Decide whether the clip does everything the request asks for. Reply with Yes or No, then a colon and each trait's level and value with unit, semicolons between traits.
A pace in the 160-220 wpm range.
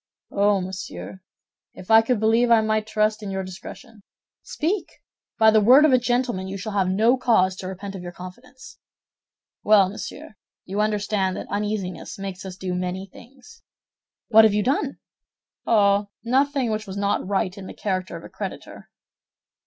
Yes: average, 170 wpm